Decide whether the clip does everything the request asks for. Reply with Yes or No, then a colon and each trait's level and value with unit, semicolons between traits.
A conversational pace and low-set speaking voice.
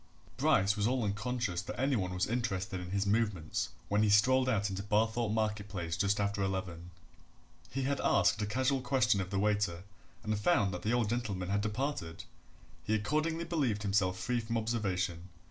Yes: average, 180 wpm; low, 105 Hz